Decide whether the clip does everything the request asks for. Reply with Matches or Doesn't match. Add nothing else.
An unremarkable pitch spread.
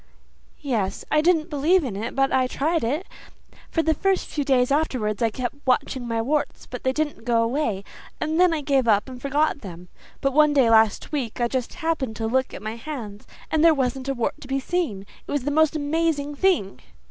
Matches